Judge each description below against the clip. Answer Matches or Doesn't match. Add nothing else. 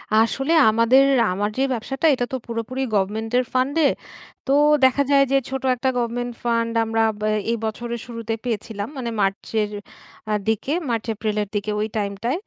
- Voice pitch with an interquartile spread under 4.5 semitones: Matches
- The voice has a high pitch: Matches